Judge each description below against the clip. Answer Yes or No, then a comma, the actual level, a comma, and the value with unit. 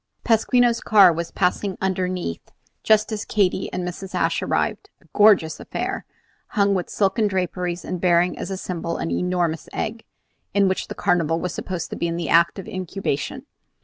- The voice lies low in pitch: No, medium, 185 Hz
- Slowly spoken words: No, average, 165 wpm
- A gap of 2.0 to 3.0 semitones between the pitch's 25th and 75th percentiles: Yes, average, 2.7 semitones